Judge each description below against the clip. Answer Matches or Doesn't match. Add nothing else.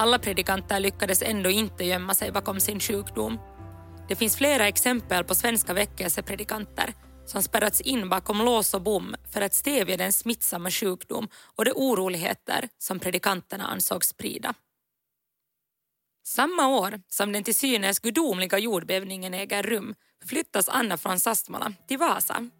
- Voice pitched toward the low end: Doesn't match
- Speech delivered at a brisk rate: Doesn't match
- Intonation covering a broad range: Doesn't match